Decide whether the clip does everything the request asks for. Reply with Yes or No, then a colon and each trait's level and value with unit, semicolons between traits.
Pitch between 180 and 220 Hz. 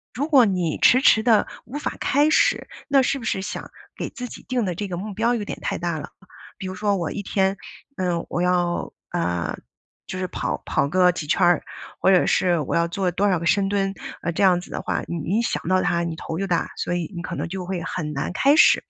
Yes: medium, 185 Hz